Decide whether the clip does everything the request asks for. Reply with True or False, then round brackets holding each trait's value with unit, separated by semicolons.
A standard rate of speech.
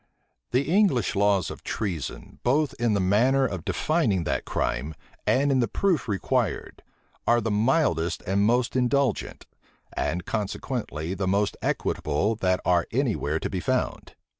True (150 wpm)